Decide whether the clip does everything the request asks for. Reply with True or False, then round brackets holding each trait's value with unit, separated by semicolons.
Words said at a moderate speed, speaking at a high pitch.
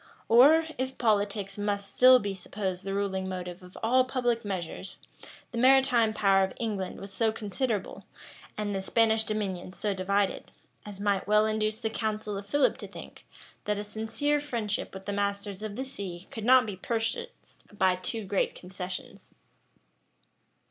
True (160 wpm; 210 Hz)